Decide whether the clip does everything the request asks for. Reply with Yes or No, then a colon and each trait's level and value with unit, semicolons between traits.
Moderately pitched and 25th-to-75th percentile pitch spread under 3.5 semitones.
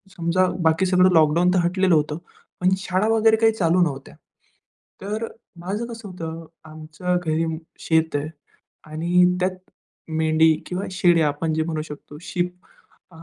Yes: medium, 170 Hz; average, 2.7 semitones